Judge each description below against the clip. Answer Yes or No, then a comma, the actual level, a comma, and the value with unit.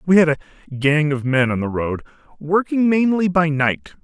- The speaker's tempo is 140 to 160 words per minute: No, average, 195 wpm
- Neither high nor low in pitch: Yes, medium, 155 Hz